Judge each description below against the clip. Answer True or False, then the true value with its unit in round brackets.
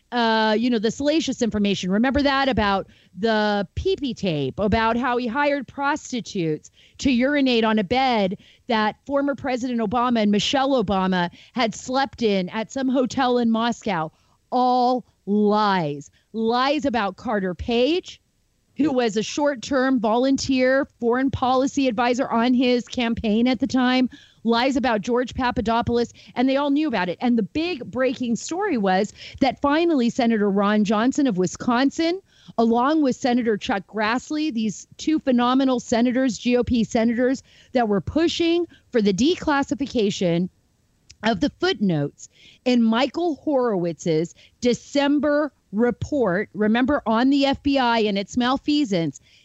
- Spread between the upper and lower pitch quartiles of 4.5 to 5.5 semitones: False (3.9 semitones)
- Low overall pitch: False (245 Hz)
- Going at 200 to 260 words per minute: False (135 wpm)